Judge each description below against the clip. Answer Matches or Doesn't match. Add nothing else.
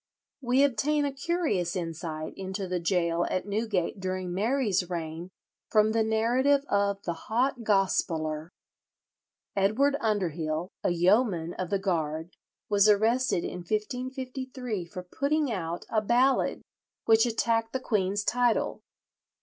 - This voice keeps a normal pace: Doesn't match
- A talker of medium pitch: Doesn't match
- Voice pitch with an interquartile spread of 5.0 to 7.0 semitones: Matches